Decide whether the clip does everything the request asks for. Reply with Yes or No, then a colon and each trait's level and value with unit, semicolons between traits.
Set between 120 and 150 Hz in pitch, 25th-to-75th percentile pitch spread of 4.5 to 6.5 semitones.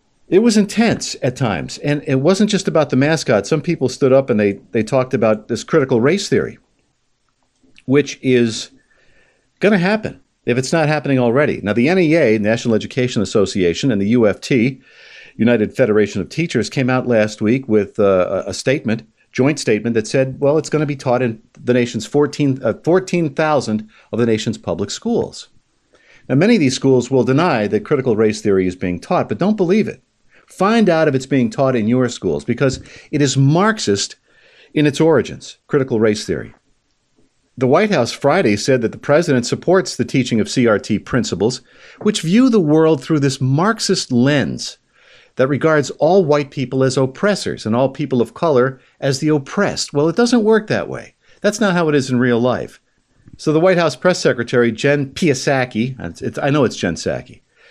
Yes: low, 135 Hz; average, 5.1 semitones